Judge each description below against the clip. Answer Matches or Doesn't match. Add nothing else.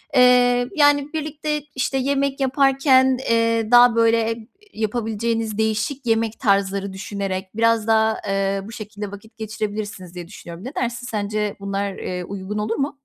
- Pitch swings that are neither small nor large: Matches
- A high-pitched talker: Matches